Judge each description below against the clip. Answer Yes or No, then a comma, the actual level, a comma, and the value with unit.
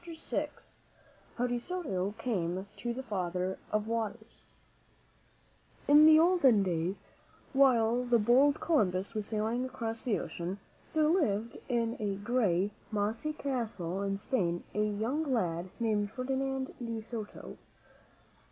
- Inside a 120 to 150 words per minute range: Yes, slow, 135 wpm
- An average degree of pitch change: Yes, average, 4.4 semitones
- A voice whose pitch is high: Yes, high, 225 Hz